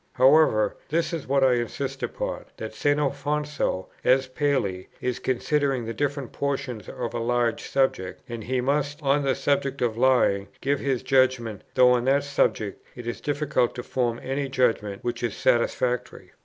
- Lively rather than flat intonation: No, average, 2.9 semitones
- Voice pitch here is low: Yes, low, 130 Hz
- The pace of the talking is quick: No, average, 170 wpm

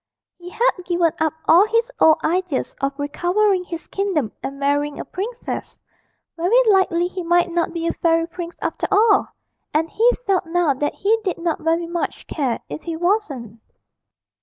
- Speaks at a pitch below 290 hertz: No, very high, 345 Hz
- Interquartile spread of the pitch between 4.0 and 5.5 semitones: No, average, 3.2 semitones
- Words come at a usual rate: Yes, average, 170 wpm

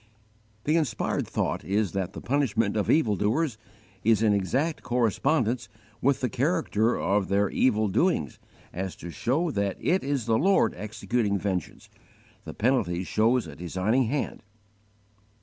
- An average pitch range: Yes, average, 4.8 semitones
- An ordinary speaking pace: Yes, average, 150 wpm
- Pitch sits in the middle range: No, low, 110 Hz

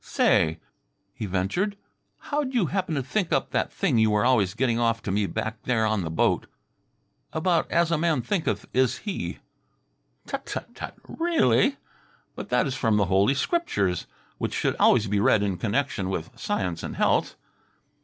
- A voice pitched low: Yes, low, 115 Hz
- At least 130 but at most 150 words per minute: No, average, 175 wpm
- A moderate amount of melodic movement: No, wide, 8.7 semitones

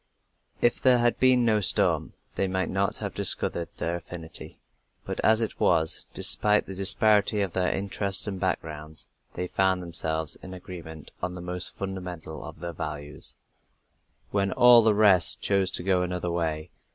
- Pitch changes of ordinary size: Yes, average, 3.1 semitones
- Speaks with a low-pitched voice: Yes, very low, 95 Hz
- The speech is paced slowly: No, average, 165 wpm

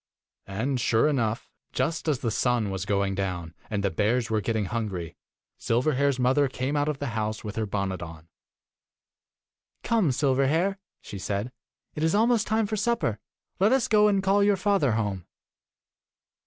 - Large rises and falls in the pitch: Yes, wide, 7.8 semitones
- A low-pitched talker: Yes, low, 125 Hz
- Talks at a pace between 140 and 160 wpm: No, average, 170 wpm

